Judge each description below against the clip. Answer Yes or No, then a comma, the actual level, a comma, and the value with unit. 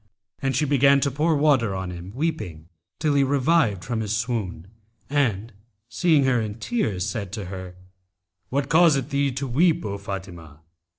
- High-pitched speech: No, low, 120 Hz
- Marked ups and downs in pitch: Yes, wide, 6.5 semitones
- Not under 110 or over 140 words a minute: No, average, 165 wpm